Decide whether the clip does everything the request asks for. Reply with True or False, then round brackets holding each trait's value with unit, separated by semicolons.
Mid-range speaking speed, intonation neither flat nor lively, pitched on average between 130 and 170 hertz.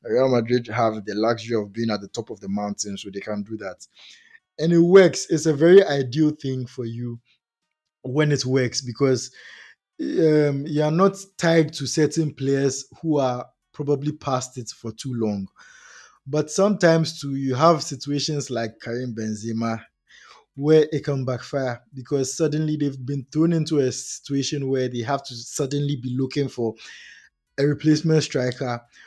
True (165 wpm; 4.1 semitones; 140 Hz)